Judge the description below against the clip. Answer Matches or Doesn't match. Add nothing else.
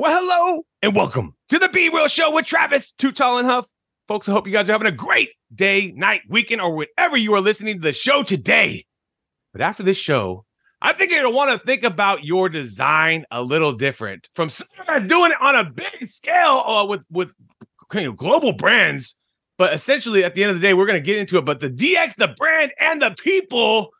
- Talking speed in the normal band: Doesn't match